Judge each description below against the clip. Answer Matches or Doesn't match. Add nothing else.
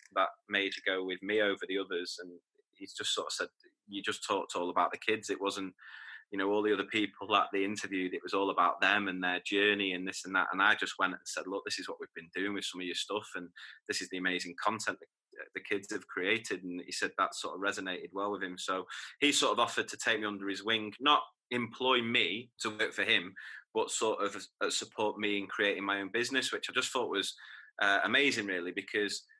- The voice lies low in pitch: Matches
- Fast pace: Matches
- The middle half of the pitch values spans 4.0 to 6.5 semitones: Matches